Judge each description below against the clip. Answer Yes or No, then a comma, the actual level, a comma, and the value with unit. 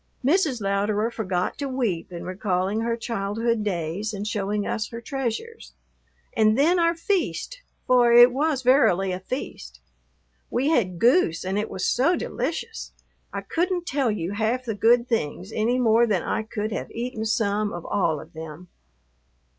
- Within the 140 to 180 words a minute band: Yes, average, 160 wpm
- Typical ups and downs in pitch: Yes, average, 4.4 semitones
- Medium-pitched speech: No, high, 220 Hz